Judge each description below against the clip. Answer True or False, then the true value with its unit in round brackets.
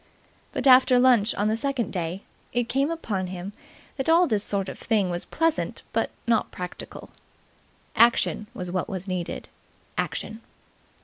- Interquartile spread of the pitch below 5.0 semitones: False (5.3 semitones)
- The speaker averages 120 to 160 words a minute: True (150 wpm)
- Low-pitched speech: False (215 Hz)